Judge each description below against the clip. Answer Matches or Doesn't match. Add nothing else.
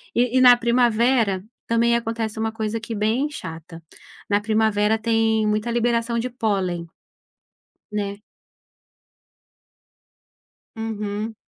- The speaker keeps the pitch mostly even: Matches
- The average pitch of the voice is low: Doesn't match